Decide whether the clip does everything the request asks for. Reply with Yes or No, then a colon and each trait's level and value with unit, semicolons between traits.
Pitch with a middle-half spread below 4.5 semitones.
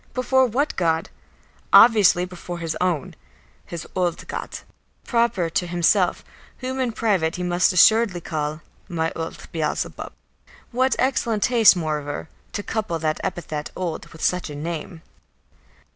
No: wide, 5.4 semitones